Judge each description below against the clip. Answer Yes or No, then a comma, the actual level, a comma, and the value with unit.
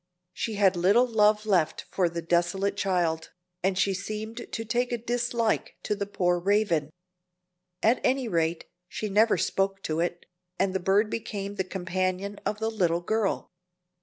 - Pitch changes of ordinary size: Yes, average, 3.5 semitones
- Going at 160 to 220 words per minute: Yes, average, 165 wpm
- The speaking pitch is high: Yes, high, 195 Hz